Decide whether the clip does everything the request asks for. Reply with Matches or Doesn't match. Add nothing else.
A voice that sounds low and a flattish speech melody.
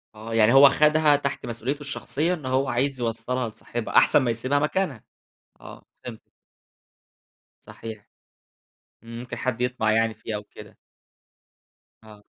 Doesn't match